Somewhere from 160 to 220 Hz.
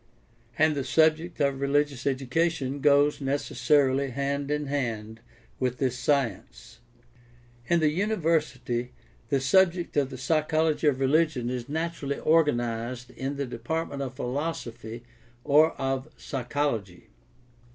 No: medium, 140 Hz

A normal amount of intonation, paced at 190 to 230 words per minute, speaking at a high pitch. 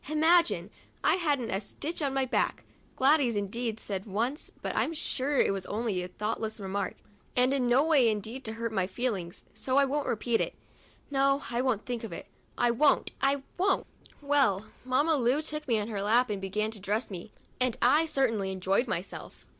Yes: average, 4.9 semitones; average, 195 wpm; high, 240 Hz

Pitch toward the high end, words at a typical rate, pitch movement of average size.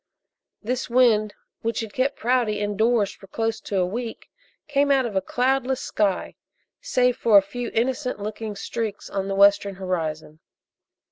Yes: high, 220 Hz; average, 155 wpm; average, 3.8 semitones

